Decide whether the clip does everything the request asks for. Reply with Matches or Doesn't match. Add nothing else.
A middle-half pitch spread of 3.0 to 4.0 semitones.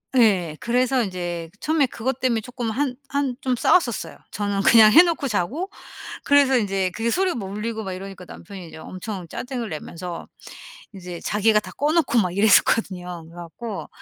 Doesn't match